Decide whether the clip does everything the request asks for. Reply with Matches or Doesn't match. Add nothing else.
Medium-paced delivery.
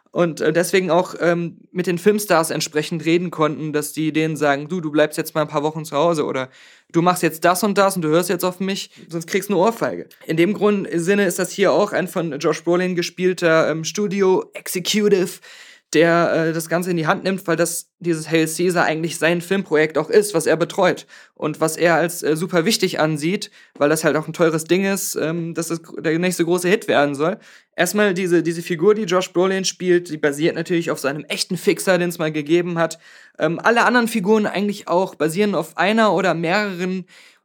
Doesn't match